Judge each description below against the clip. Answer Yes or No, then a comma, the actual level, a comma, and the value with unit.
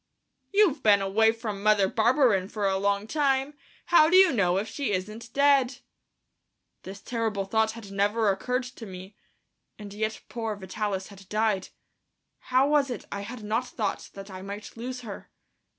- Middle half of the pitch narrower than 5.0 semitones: Yes, average, 4.0 semitones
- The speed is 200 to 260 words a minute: No, average, 165 wpm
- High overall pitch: Yes, high, 215 Hz